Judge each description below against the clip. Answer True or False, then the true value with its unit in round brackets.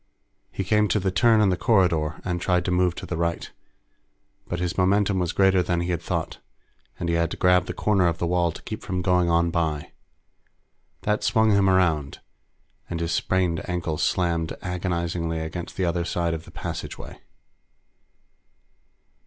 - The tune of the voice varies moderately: False (1.8 semitones)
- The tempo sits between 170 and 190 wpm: True (180 wpm)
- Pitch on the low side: True (90 Hz)